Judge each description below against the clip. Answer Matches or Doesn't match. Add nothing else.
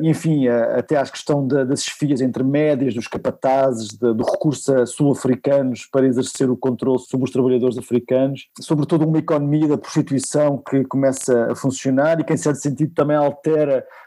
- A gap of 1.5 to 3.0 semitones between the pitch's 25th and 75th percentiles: Matches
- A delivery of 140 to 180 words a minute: Matches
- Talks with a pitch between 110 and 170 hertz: Matches